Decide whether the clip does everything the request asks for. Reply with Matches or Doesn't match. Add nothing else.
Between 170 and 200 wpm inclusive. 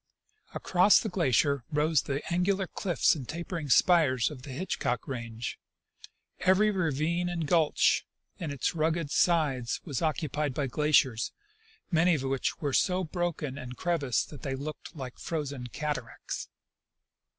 Doesn't match